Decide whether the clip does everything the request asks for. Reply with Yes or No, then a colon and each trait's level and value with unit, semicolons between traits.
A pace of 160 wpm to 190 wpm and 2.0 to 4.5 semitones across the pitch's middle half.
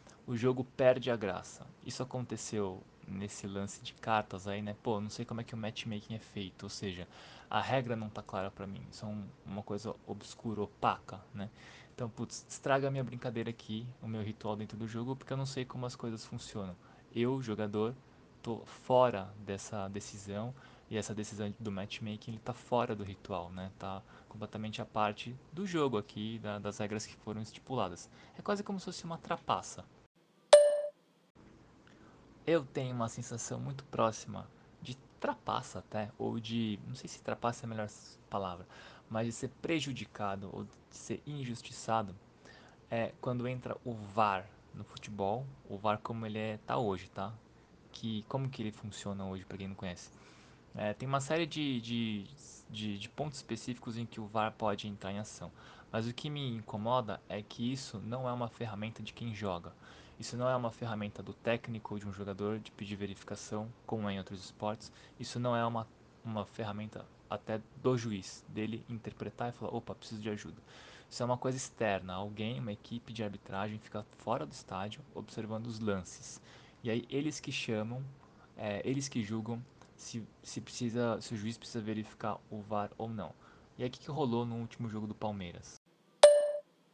Yes: fast, 185 wpm; average, 2.9 semitones